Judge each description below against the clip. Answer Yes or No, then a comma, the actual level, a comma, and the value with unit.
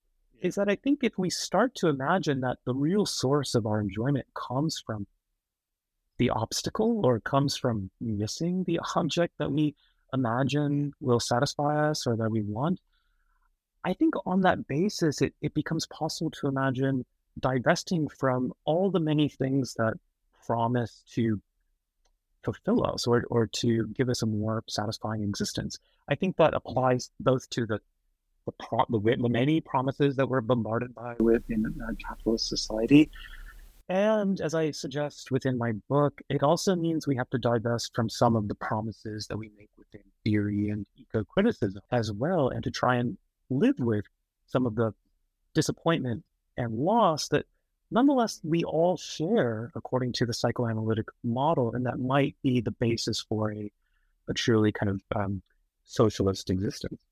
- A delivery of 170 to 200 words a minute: No, average, 160 wpm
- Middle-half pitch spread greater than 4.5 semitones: Yes, average, 5.3 semitones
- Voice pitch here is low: Yes, low, 125 Hz